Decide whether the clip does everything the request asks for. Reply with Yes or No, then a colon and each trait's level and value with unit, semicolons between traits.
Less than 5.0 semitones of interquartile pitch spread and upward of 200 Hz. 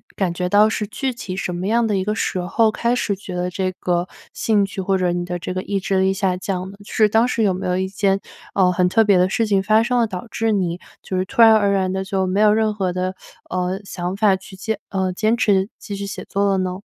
No: narrow, 2.5 semitones; high, 195 Hz